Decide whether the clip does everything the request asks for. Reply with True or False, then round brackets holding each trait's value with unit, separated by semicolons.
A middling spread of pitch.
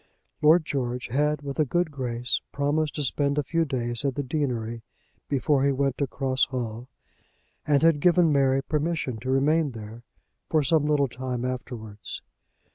True (3.1 semitones)